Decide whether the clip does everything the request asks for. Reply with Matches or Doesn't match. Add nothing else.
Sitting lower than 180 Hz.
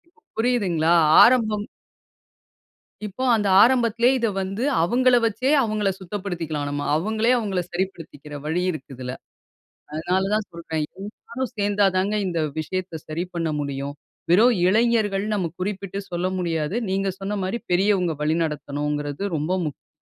Doesn't match